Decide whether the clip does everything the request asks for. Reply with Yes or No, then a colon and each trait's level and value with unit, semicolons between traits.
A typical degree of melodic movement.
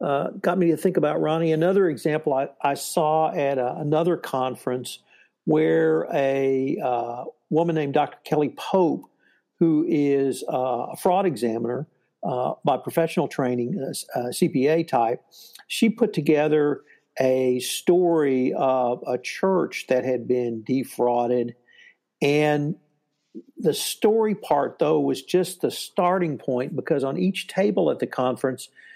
Yes: average, 4.6 semitones